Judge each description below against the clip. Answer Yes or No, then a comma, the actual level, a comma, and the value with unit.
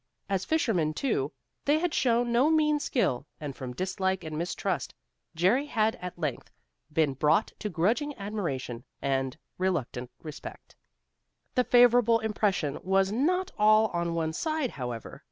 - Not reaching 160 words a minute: Yes, average, 140 wpm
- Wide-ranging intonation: Yes, wide, 7.9 semitones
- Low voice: No, high, 190 Hz